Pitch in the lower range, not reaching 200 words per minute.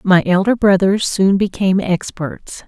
No: high, 190 Hz; slow, 135 wpm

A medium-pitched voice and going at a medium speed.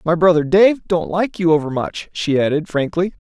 Yes: medium, 170 Hz; average, 185 wpm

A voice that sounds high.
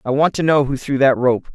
No: low, 135 Hz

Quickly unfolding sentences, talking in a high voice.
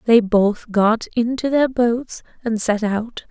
No: average, 165 wpm; high, 225 Hz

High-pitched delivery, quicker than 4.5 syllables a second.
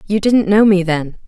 Yes: high, 195 Hz; 4.9 syllables/s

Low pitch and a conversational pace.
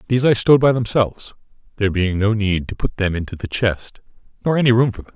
No: low, 110 Hz; fast, 235 wpm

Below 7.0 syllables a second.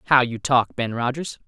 Yes: 5.0 syllables/s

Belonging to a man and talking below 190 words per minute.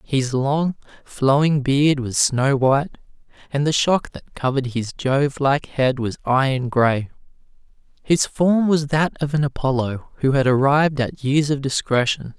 Yes: male; average, 160 wpm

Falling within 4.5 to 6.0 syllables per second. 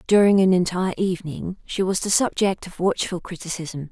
Yes: 5.5 syllables/s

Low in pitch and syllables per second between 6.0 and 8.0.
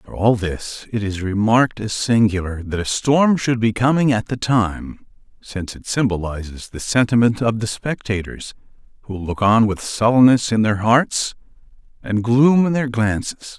No: low, 110 Hz; 4.6 syllables/s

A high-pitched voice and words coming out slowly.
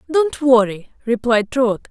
Yes: very high, 250 Hz; slow, 125 wpm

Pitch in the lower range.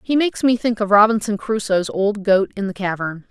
No: high, 205 Hz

